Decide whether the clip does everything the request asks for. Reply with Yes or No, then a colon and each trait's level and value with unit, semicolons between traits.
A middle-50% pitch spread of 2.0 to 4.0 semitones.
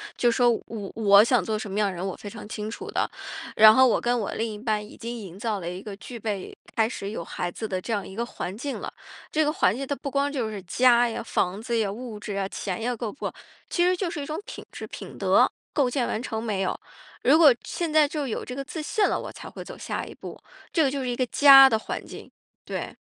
No: average, 4.5 semitones